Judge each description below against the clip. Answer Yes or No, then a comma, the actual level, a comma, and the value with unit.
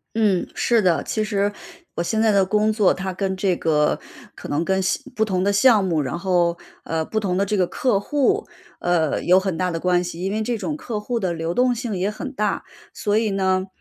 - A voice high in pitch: Yes, high, 195 Hz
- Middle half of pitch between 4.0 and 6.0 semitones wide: No, average, 3.3 semitones